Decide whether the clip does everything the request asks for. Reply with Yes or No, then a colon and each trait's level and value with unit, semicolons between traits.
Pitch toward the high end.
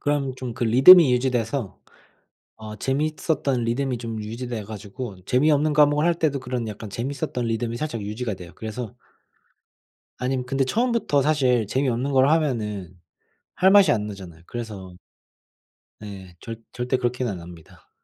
No: low, 125 Hz